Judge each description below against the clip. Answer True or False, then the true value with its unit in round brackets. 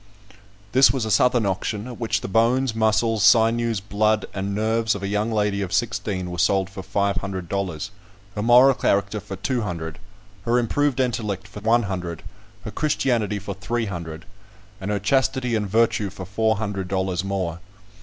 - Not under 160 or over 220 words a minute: True (175 wpm)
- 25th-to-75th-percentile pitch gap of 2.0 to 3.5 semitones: True (3.1 semitones)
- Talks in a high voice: False (105 Hz)